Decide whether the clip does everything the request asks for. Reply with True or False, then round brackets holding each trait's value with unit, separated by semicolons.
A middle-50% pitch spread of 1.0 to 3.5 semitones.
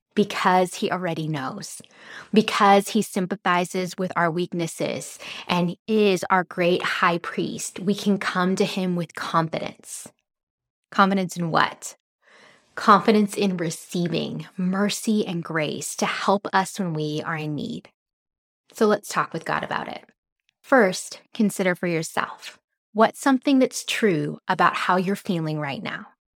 True (2.9 semitones)